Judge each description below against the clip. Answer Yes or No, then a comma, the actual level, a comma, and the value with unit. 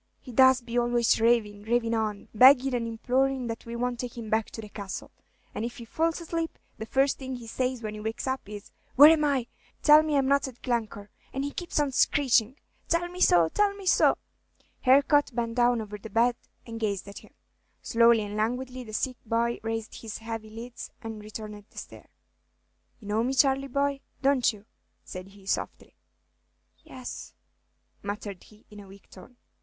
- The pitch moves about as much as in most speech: Yes, average, 3.5 semitones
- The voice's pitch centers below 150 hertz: No, high, 235 Hz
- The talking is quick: No, average, 190 wpm